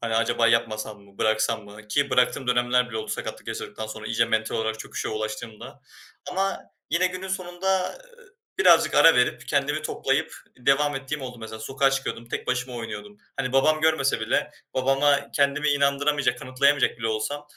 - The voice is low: Yes, low, 130 Hz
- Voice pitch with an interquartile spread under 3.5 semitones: No, average, 4.6 semitones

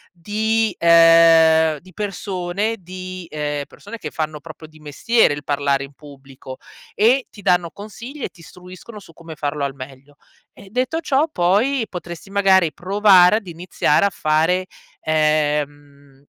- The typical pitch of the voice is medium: Yes, medium, 170 Hz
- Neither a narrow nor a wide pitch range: Yes, average, 5.0 semitones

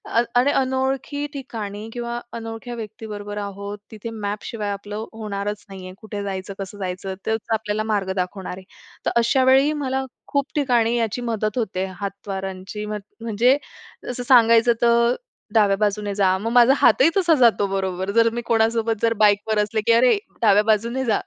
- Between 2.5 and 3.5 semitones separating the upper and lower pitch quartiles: Yes, average, 2.8 semitones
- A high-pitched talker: Yes, high, 220 Hz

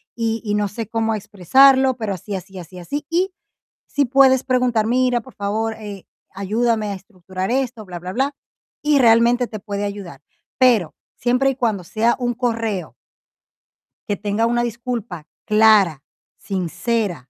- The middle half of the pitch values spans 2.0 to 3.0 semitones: No, average, 3.7 semitones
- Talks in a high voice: Yes, high, 220 Hz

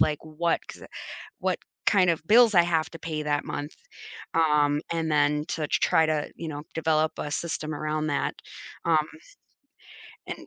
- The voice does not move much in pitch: Yes, narrow, 1.7 semitones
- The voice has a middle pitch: Yes, medium, 155 Hz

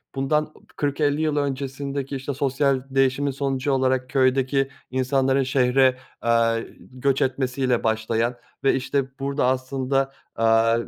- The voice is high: No, low, 135 Hz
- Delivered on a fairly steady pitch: Yes, narrow, 1.4 semitones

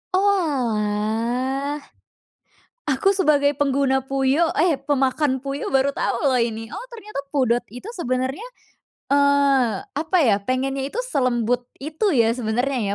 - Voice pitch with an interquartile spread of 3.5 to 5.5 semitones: No, average, 2.8 semitones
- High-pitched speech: Yes, very high, 270 Hz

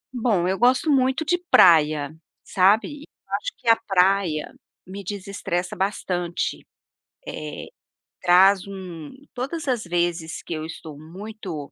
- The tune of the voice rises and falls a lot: No, average, 4.4 semitones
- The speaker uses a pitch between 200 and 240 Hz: No, high, 190 Hz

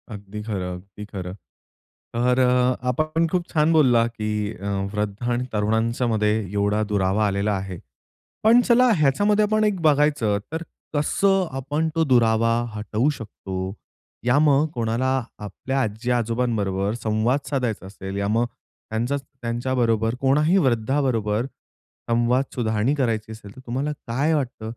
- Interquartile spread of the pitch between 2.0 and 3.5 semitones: No, average, 4.6 semitones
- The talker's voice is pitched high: No, low, 120 Hz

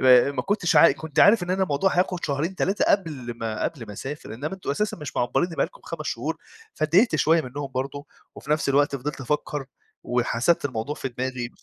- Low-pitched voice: No, medium, 145 Hz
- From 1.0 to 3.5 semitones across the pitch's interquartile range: No, average, 4.8 semitones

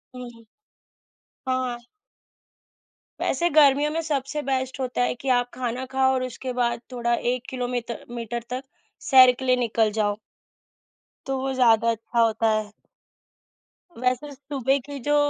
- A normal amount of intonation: No, narrow, 2.1 semitones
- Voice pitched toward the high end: Yes, very high, 250 Hz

